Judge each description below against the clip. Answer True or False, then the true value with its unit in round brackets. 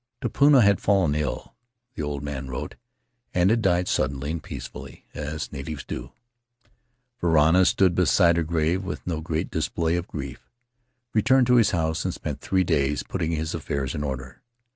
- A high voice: False (80 Hz)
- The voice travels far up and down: False (4.1 semitones)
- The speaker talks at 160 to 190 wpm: True (165 wpm)